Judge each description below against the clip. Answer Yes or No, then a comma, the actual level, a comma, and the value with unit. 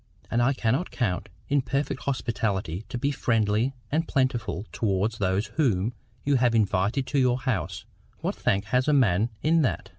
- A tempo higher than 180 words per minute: No, average, 160 wpm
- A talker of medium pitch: No, low, 120 Hz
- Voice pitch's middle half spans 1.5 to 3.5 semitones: No, average, 4.8 semitones